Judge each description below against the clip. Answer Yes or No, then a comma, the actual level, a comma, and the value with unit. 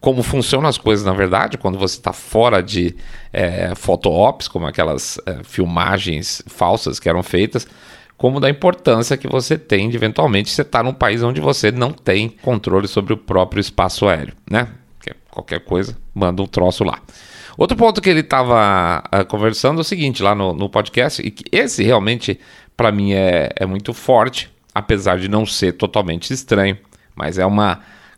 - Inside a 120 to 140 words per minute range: No, average, 180 wpm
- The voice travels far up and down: No, average, 4.1 semitones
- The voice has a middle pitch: No, low, 105 Hz